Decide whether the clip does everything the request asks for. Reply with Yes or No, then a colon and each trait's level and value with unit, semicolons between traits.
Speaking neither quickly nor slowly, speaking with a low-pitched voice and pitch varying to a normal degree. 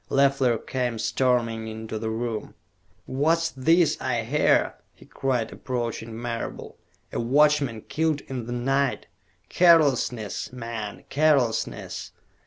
No: slow, 110 wpm; low, 125 Hz; average, 3.4 semitones